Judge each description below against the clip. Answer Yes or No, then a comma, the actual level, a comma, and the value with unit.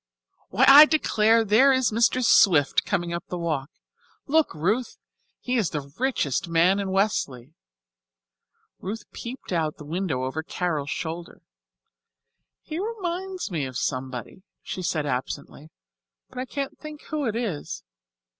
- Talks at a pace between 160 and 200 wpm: No, average, 145 wpm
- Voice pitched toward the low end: No, high, 190 Hz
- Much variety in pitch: Yes, wide, 8.7 semitones